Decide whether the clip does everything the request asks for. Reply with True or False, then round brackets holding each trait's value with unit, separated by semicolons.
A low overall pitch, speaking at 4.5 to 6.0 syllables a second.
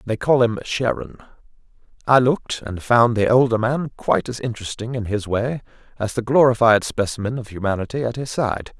True (115 Hz; 5.5 syllables/s)